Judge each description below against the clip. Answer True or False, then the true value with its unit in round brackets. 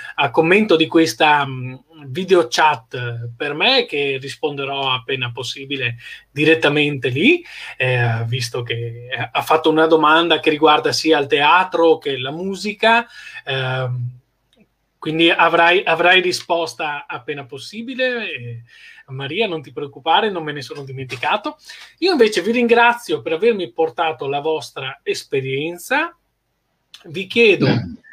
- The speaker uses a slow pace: False (125 wpm)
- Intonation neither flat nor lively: False (5.8 semitones)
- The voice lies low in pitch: False (155 Hz)